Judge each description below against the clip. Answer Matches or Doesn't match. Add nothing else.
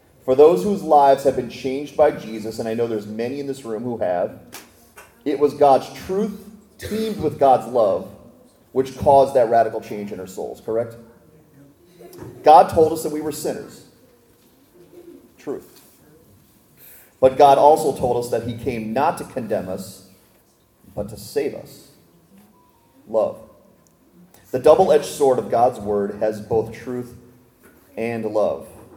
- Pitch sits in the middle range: Doesn't match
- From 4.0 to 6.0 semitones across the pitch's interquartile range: Matches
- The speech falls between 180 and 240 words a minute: Doesn't match